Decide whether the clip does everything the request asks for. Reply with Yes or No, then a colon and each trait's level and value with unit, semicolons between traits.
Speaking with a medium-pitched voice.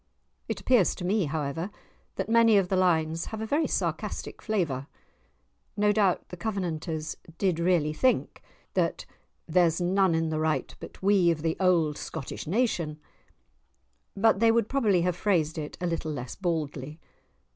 Yes: medium, 175 Hz